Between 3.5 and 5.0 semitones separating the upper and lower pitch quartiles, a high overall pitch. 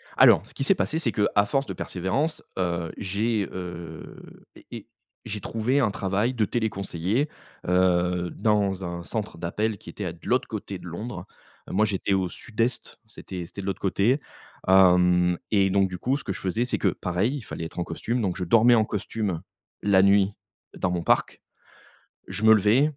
No: average, 3.9 semitones; low, 100 Hz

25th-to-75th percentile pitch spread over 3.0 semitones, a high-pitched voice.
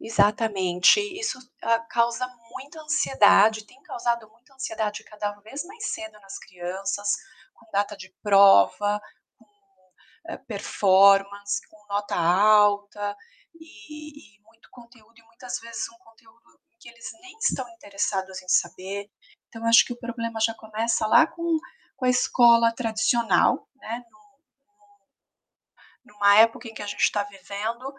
No: average, 2.7 semitones; high, 220 Hz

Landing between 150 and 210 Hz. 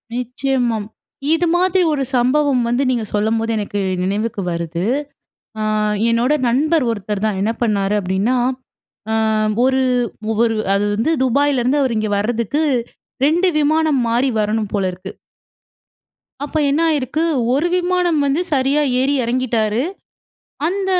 No: very high, 250 Hz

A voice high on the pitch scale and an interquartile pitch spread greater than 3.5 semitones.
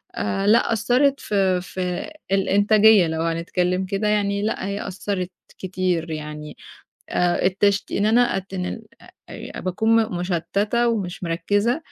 No: high, 195 Hz; average, 2.9 semitones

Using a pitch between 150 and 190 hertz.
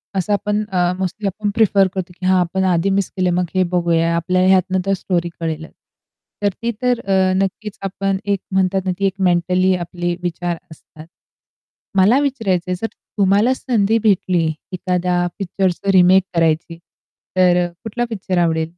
Yes: medium, 185 Hz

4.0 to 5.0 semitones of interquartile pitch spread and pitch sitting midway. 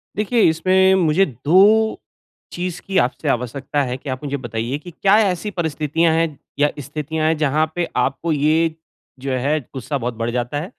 Yes: average, 4.5 semitones; medium, 155 Hz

